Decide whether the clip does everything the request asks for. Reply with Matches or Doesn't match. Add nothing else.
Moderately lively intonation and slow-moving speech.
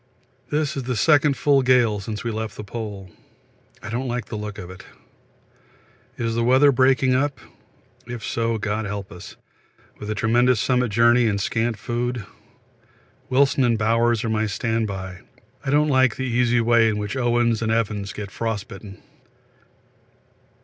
Doesn't match